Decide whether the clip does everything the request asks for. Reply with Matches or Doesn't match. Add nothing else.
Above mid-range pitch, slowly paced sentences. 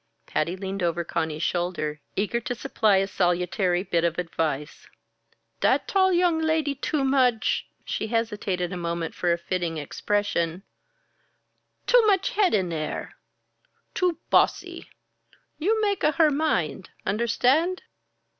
Matches